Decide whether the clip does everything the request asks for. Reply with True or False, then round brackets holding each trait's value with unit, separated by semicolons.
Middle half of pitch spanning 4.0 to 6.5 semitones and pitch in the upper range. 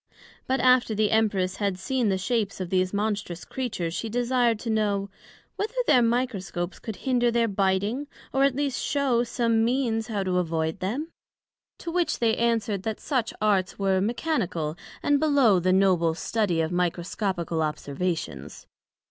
True (4.7 semitones; 210 Hz)